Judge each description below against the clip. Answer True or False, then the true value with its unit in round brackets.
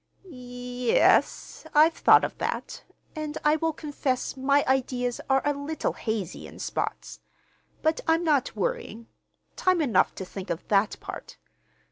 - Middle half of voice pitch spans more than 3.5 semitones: True (4.2 semitones)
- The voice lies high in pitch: True (270 Hz)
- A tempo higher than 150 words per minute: False (145 wpm)